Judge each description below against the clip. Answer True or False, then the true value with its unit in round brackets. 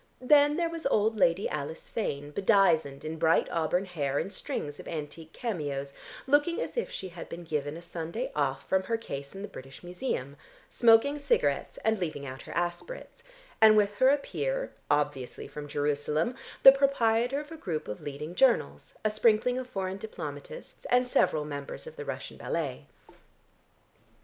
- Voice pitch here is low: False (180 Hz)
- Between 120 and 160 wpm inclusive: False (170 wpm)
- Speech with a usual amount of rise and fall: False (8.6 semitones)